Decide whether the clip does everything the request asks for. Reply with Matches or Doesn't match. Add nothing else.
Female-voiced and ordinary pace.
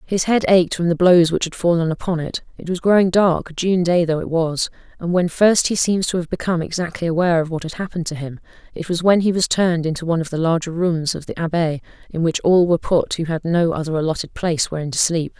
Doesn't match